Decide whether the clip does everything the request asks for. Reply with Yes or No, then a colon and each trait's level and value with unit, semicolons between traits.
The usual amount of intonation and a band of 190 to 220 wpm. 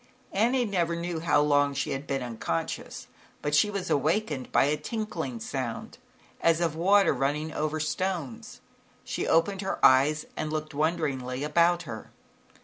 No: average, 3.8 semitones; average, 150 wpm